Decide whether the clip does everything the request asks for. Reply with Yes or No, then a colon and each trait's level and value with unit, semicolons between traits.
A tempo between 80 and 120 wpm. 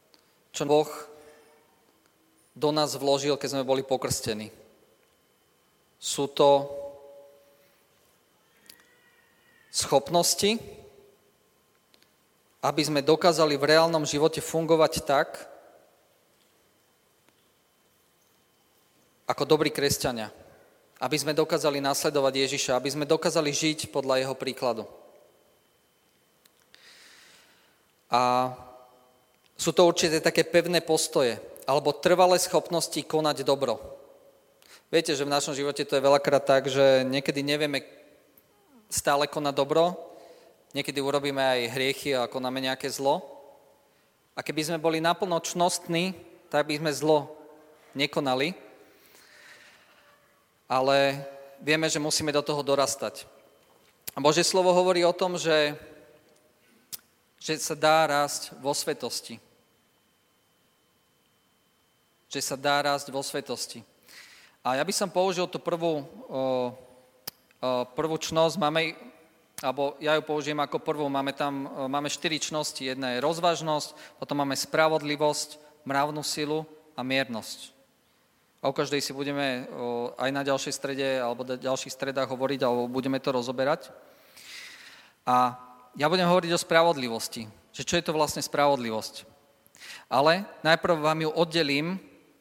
Yes: average, 115 wpm